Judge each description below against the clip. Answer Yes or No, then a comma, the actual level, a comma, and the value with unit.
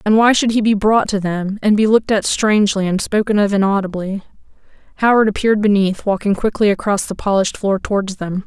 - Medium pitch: No, high, 205 Hz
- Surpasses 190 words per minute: Yes, average, 200 wpm